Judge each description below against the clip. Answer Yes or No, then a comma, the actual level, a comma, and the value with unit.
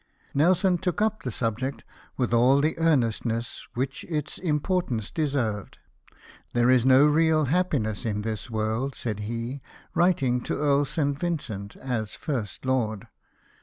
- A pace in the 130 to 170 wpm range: Yes, average, 140 wpm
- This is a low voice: Yes, low, 130 Hz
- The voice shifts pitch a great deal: No, average, 5.0 semitones